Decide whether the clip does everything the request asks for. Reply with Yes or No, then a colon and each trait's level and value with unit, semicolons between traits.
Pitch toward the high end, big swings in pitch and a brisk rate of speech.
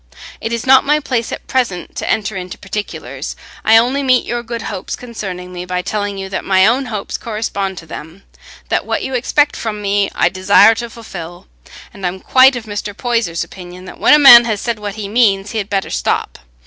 No: high, 210 Hz; average, 3.8 semitones; fast, 210 wpm